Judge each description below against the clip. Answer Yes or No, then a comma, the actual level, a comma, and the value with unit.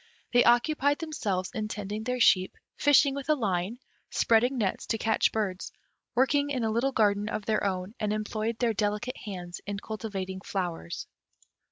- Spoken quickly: No, average, 165 wpm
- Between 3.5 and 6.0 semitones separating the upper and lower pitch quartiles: Yes, average, 3.8 semitones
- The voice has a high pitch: Yes, high, 215 Hz